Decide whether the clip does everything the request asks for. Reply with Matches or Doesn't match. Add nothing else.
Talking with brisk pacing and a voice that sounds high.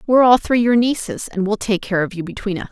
Matches